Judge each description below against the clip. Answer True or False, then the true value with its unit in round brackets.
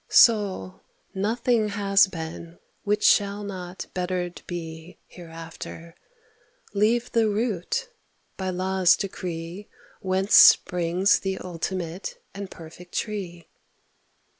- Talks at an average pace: False (105 wpm)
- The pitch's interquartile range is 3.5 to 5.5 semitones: False (2.9 semitones)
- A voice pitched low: False (185 Hz)